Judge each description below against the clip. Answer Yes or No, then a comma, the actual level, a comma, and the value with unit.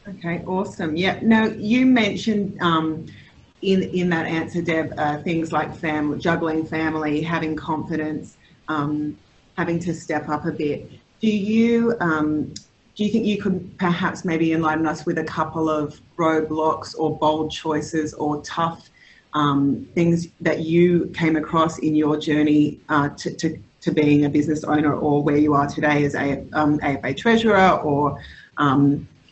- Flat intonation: Yes, narrow, 2.3 semitones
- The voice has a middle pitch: Yes, medium, 160 Hz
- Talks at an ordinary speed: Yes, average, 160 wpm